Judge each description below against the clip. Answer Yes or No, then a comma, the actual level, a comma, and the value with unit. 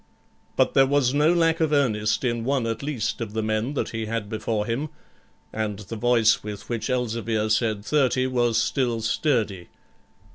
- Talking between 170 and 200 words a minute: Yes, average, 175 wpm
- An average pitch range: Yes, average, 3.4 semitones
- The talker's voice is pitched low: Yes, low, 115 Hz